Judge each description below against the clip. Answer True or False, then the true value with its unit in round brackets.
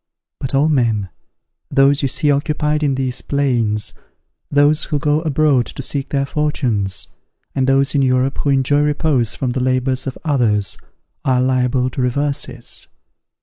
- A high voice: False (135 Hz)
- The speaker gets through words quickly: False (150 wpm)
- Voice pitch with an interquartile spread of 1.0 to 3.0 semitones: True (2.4 semitones)